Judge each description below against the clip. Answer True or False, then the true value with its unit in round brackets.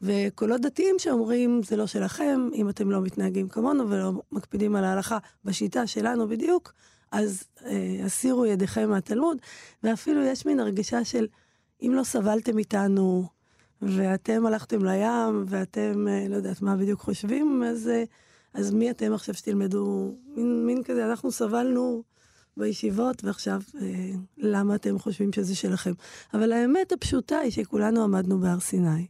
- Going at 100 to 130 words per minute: False (145 wpm)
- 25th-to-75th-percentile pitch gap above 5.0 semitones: False (3.4 semitones)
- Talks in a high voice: True (215 Hz)